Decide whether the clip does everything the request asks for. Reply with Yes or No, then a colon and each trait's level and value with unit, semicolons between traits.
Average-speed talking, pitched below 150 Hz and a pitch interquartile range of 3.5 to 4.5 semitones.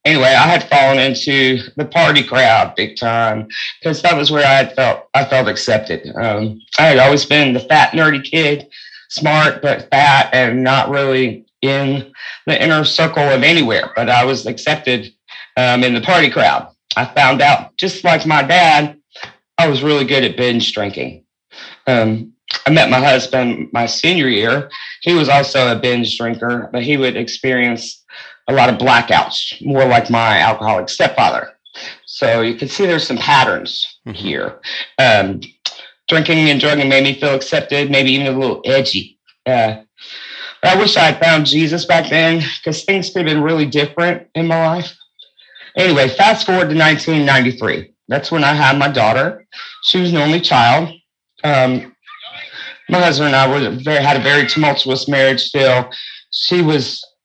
Yes: average, 170 wpm; medium, 140 Hz; average, 3.9 semitones